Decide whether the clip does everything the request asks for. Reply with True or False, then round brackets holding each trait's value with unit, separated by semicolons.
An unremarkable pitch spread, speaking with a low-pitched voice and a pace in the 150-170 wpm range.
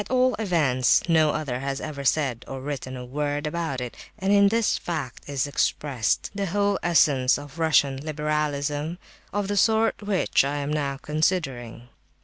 False (4.2 semitones; 150 Hz; 165 wpm)